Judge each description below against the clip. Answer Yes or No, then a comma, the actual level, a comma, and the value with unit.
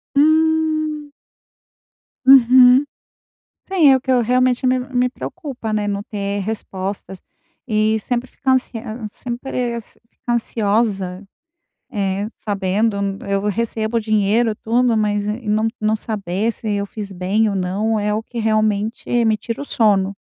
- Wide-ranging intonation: No, average, 3.5 semitones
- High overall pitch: Yes, high, 220 Hz